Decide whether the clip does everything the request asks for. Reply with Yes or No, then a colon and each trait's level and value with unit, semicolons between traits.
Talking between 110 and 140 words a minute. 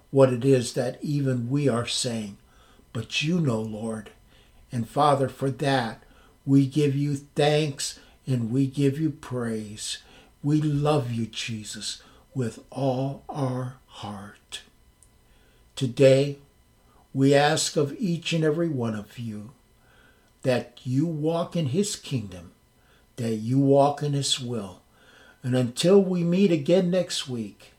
Yes: slow, 135 wpm